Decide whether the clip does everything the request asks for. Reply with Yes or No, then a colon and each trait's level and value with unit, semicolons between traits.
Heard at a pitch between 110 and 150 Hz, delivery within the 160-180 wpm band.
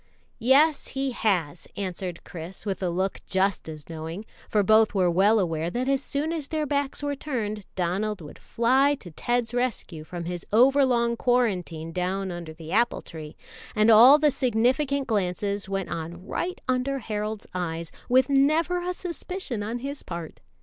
No: high, 215 Hz; average, 165 wpm